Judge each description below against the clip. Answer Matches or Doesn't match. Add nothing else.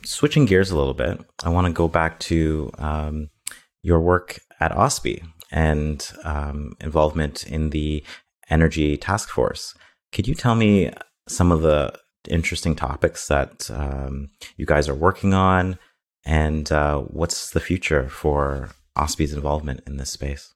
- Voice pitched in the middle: Doesn't match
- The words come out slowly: Doesn't match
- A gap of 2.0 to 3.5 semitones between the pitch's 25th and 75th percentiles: Matches